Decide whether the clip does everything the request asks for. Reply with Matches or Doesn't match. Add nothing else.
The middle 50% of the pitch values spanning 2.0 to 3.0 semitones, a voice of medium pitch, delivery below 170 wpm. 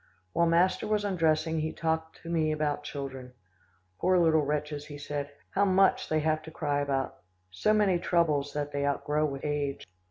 Doesn't match